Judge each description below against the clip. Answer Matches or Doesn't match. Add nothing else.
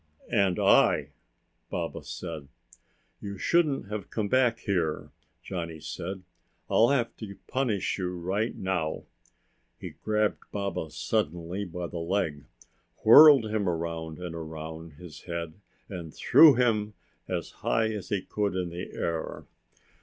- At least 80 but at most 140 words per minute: Matches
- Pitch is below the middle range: Matches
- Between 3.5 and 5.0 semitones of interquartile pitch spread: Matches